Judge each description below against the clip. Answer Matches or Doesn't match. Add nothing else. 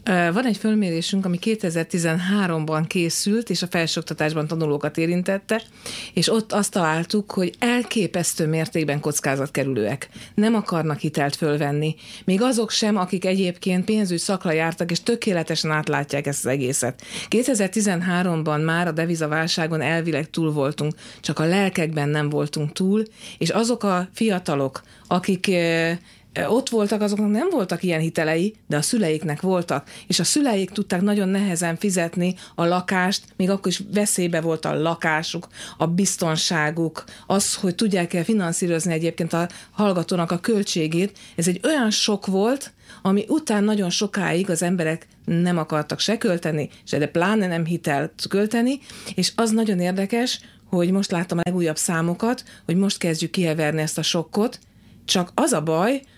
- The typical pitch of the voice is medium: Matches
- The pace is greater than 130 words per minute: Matches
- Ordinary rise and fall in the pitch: Matches